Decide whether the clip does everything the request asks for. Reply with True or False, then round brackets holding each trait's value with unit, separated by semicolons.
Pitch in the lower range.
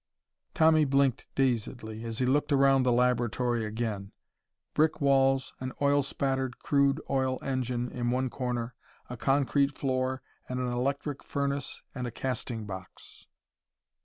True (130 Hz)